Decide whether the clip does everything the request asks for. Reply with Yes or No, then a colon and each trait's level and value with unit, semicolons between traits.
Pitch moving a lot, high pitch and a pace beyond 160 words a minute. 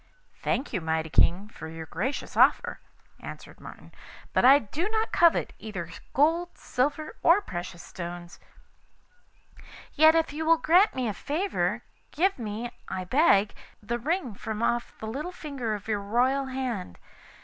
No: wide, 7.6 semitones; very high, 250 Hz; average, 155 wpm